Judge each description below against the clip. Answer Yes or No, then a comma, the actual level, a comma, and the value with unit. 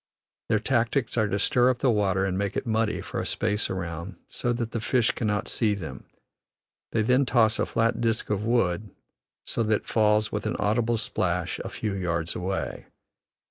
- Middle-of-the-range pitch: No, low, 110 Hz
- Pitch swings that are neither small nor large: Yes, average, 3.1 semitones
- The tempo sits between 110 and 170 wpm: No, average, 190 wpm